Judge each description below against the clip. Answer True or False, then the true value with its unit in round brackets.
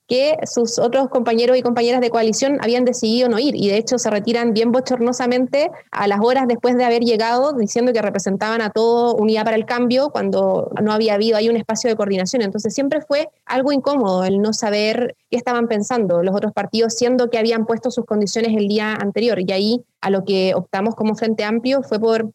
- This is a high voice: True (230 Hz)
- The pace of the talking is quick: True (210 wpm)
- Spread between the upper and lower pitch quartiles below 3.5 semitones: True (2.5 semitones)